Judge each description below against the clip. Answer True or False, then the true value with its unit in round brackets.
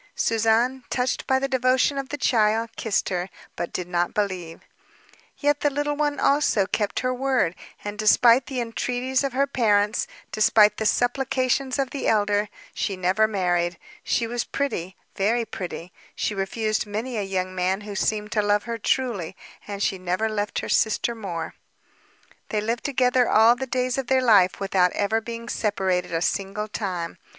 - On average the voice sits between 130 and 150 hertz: False (220 Hz)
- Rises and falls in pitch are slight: False (4.4 semitones)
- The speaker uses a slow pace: False (170 wpm)